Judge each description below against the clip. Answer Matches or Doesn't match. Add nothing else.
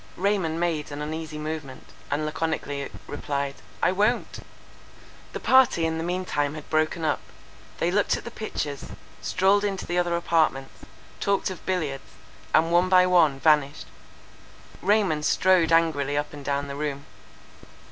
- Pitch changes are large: Doesn't match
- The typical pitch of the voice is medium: Matches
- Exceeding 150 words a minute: Doesn't match